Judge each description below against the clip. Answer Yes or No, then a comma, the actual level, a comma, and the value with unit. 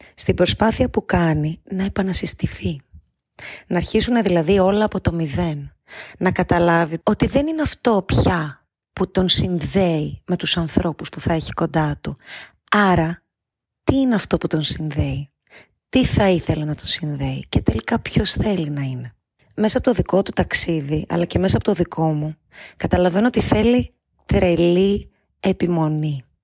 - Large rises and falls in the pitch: No, average, 4.0 semitones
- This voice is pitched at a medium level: Yes, medium, 175 Hz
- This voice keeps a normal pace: Yes, average, 155 wpm